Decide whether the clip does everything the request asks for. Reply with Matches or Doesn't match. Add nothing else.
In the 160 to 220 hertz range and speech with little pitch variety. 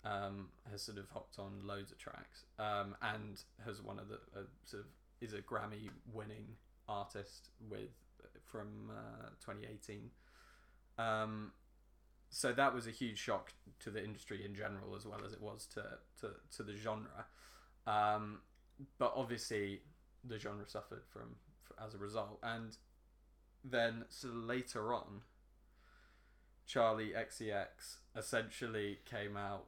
Doesn't match